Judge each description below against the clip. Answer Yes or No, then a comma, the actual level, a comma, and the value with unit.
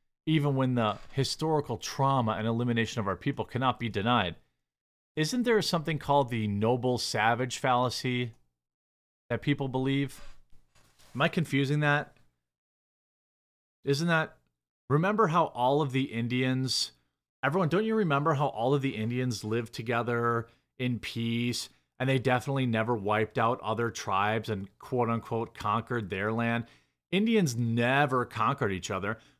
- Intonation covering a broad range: No, average, 4.1 semitones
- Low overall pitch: Yes, low, 120 Hz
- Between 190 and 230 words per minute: No, average, 140 wpm